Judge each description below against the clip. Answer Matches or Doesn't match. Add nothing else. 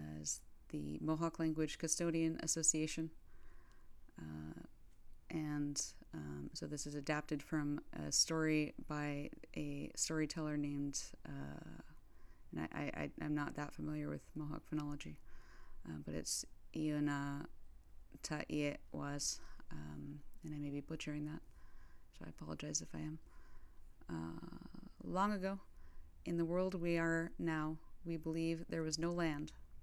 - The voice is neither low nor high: Matches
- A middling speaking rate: Doesn't match